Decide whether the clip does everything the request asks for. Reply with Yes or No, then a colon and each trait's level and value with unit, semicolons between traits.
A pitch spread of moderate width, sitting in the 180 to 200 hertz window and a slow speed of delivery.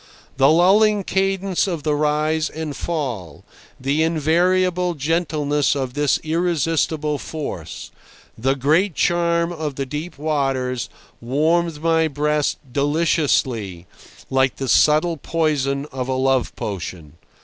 No: average, 3.7 semitones; medium, 150 Hz; slow, 115 wpm